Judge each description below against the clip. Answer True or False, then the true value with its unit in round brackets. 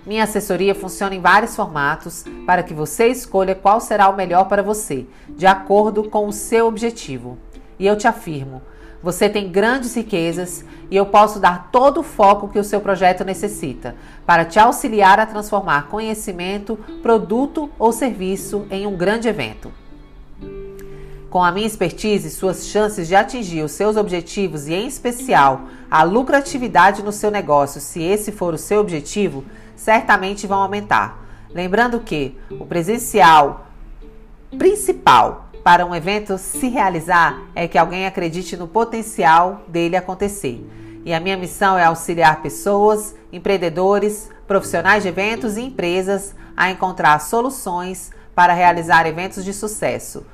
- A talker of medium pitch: False (195 Hz)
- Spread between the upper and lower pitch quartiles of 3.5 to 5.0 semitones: True (3.8 semitones)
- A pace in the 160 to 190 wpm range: False (145 wpm)